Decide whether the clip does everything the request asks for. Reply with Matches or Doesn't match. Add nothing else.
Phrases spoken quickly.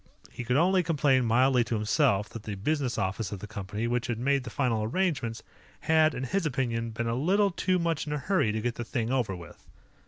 Matches